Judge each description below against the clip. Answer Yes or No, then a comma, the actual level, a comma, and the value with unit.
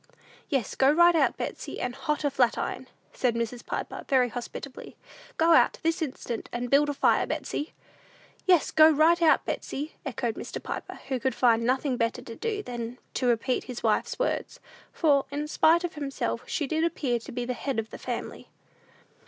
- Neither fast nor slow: Yes, average, 185 wpm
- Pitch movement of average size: Yes, average, 4.3 semitones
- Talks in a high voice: Yes, very high, 270 Hz